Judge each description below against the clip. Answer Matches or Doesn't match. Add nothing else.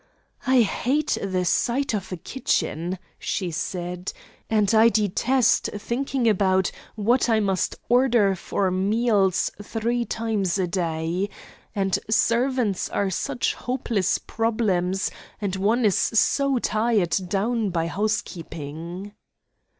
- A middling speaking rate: Doesn't match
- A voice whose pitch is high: Matches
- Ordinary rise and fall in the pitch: Matches